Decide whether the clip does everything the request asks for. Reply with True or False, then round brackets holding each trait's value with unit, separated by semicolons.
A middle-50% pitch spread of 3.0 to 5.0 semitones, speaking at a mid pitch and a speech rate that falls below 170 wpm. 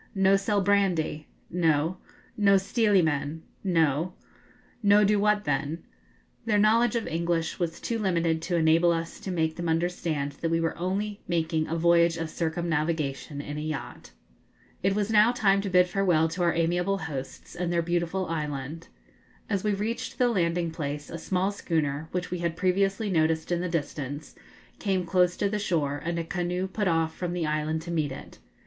False (3.3 semitones; 170 Hz; 180 wpm)